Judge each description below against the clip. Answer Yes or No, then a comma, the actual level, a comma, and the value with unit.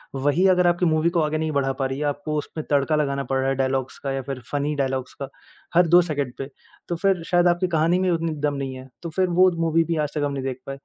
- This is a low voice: No, medium, 150 Hz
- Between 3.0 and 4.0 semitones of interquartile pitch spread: Yes, average, 3.7 semitones